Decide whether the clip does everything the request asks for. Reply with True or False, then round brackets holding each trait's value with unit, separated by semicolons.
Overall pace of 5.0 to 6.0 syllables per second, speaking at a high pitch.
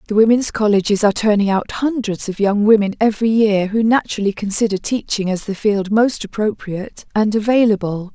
True (5.6 syllables/s; 210 Hz)